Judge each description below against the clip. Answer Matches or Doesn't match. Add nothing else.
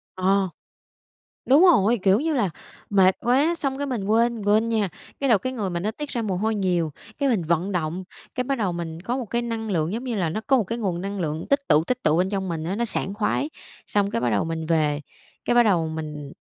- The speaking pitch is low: Doesn't match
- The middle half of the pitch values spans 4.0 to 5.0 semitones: Doesn't match